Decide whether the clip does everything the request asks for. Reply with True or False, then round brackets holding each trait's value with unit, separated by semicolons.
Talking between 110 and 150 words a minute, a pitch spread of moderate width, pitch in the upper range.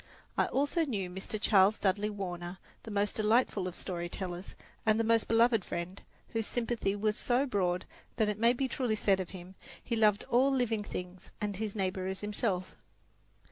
False (180 wpm; 3.4 semitones; 210 Hz)